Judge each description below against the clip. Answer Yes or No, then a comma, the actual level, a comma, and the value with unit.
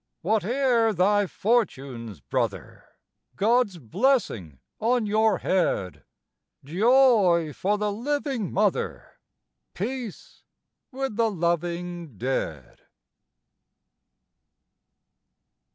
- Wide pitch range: Yes, wide, 5.7 semitones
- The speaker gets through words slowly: Yes, slow, 70 wpm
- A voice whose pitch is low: No, high, 205 Hz